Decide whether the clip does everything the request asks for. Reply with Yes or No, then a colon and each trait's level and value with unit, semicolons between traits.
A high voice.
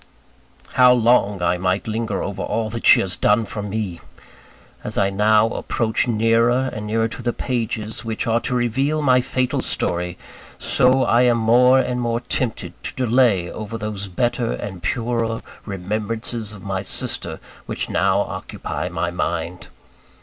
No: low, 110 Hz